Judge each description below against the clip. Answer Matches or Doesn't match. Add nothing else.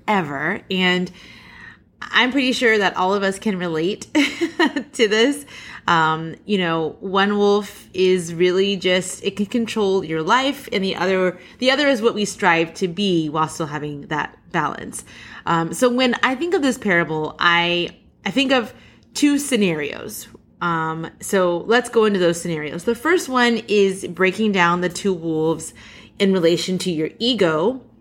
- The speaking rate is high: Doesn't match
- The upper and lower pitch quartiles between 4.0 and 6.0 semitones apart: Matches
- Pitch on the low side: Doesn't match